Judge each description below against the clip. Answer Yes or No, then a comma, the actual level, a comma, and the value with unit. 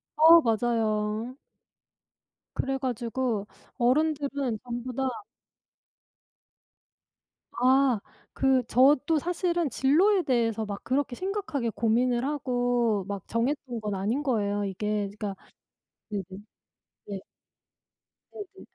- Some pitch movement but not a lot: Yes, average, 4.4 semitones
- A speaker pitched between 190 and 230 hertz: No, high, 245 Hz